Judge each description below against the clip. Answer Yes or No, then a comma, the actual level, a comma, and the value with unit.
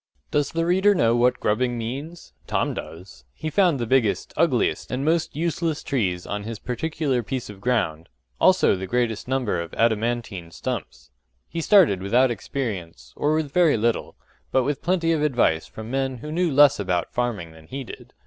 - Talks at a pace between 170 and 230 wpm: Yes, average, 175 wpm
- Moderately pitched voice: No, low, 125 Hz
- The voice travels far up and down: Yes, wide, 6.4 semitones